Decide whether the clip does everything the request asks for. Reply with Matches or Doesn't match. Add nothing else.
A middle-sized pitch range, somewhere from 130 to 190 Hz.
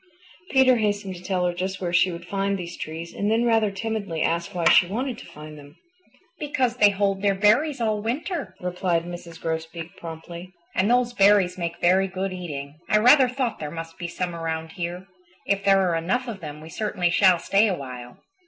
Matches